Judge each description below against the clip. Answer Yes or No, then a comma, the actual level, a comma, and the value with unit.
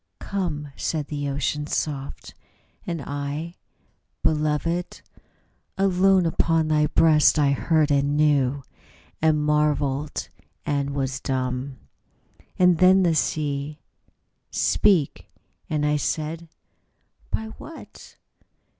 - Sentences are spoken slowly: Yes, slow, 115 wpm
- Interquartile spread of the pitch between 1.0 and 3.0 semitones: Yes, narrow, 2.5 semitones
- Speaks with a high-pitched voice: No, medium, 150 Hz